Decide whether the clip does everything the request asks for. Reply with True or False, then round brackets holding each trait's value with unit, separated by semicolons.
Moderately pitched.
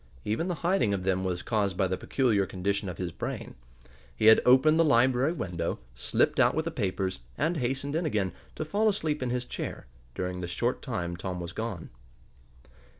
False (110 Hz)